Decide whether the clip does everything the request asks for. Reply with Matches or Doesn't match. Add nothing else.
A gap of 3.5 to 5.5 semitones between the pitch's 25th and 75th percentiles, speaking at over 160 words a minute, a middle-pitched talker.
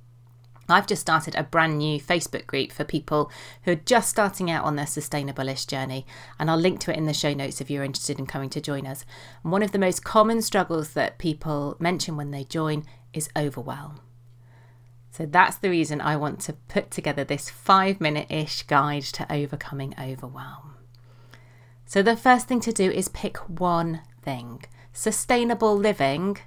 Matches